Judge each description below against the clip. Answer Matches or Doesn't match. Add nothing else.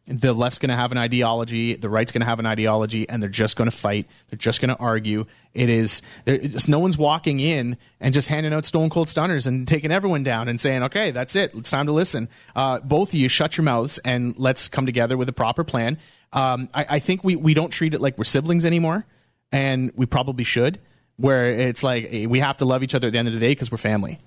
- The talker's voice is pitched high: Doesn't match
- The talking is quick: Matches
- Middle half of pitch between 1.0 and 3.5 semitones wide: Doesn't match